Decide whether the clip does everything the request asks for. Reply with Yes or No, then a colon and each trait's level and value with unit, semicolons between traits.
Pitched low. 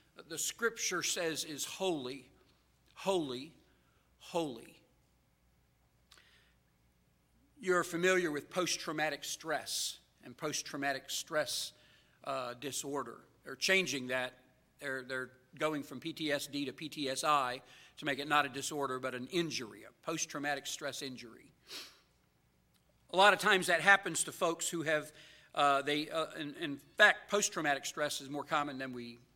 No: medium, 145 Hz